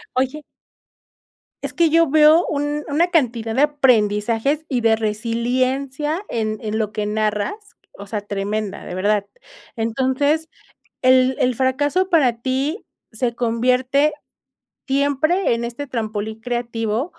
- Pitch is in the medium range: No, very high, 255 Hz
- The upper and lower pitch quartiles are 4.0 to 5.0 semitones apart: Yes, average, 4.6 semitones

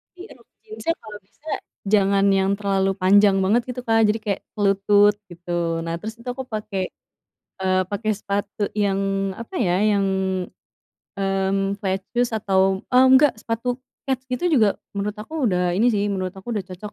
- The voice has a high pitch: Yes, high, 200 Hz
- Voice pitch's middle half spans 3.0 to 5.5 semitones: No, narrow, 2.5 semitones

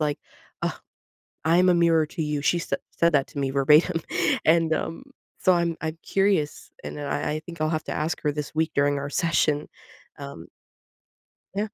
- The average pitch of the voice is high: No, medium, 155 Hz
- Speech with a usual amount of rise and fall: No, narrow, 2.3 semitones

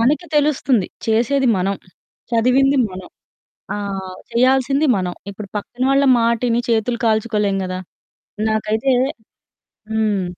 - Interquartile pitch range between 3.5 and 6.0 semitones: Yes, average, 4.3 semitones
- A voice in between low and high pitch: No, high, 225 Hz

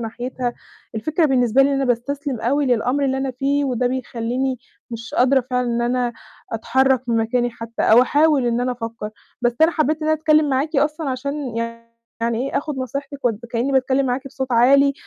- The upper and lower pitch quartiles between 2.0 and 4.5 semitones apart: Yes, narrow, 2.6 semitones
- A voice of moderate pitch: No, very high, 260 Hz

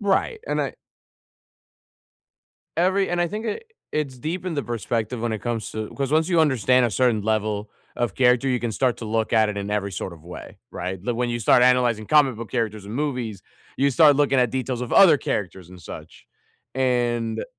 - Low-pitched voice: Yes, low, 120 Hz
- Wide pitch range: No, average, 4.2 semitones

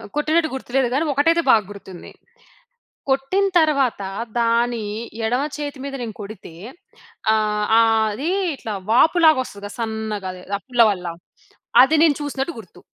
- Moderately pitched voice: No, high, 245 Hz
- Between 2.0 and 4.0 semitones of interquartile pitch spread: No, average, 5.0 semitones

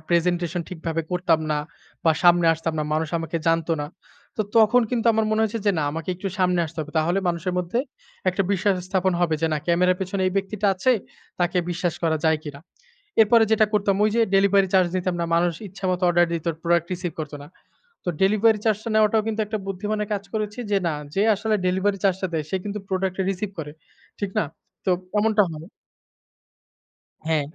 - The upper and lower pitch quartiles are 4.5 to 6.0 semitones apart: No, average, 3.4 semitones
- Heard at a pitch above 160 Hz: Yes, medium, 185 Hz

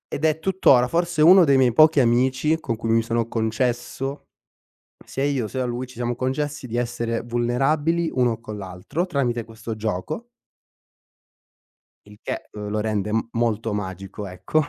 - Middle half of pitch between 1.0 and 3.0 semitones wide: No, average, 4.0 semitones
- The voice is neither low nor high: No, low, 120 Hz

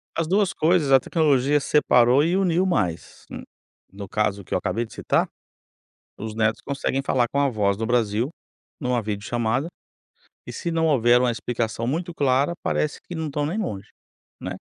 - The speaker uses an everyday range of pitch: No, wide, 5.8 semitones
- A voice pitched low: Yes, low, 130 Hz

